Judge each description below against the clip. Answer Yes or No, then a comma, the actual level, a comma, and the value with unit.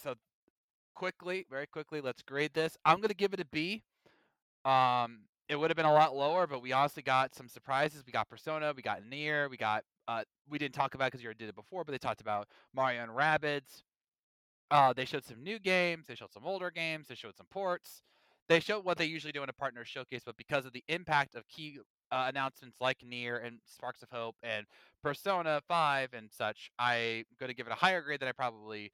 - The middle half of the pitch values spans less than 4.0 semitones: No, average, 4.4 semitones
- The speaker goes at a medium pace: No, fast, 230 wpm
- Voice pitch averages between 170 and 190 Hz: No, low, 135 Hz